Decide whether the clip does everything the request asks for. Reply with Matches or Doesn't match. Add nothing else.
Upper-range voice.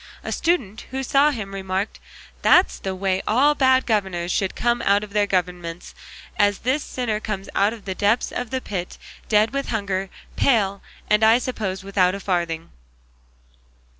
Matches